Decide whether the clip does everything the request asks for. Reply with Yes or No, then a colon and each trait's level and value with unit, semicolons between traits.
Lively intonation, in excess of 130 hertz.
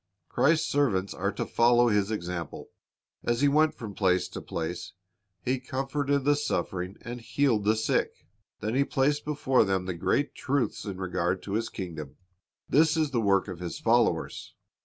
No: wide, 6.9 semitones; low, 110 Hz